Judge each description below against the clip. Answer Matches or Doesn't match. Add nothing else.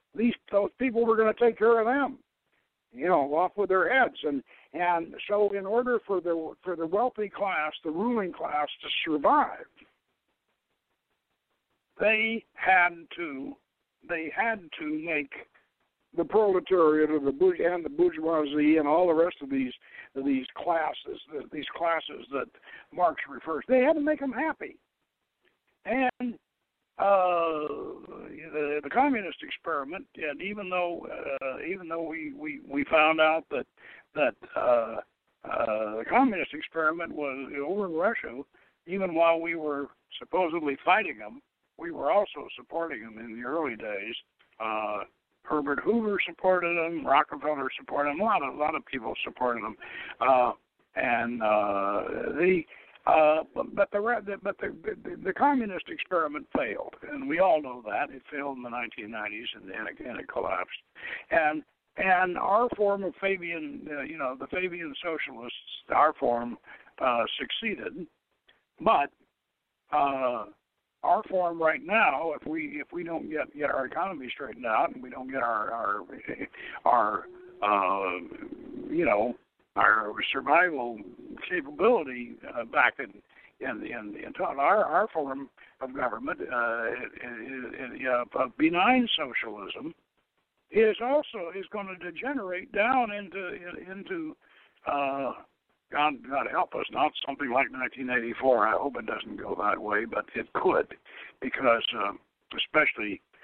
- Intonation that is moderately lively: Doesn't match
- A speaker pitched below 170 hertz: Doesn't match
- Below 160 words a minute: Matches